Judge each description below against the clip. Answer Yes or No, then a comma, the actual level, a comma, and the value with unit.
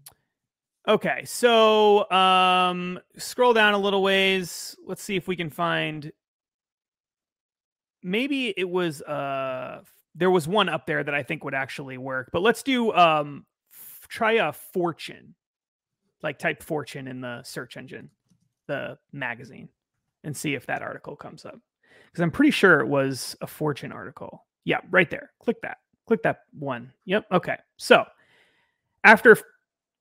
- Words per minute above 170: No, average, 150 wpm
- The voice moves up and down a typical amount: No, wide, 5.9 semitones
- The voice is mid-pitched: Yes, medium, 180 Hz